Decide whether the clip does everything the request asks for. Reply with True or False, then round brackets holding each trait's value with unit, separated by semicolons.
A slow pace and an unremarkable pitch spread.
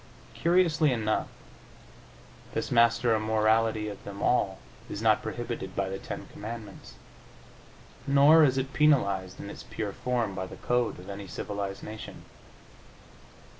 True (130 wpm; 3.7 semitones)